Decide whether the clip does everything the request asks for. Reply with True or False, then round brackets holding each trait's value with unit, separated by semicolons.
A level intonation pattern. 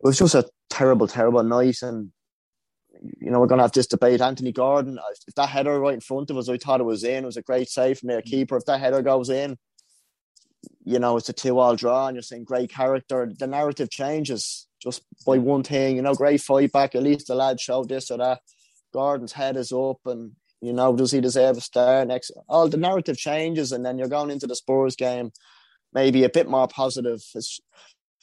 True (1.5 semitones)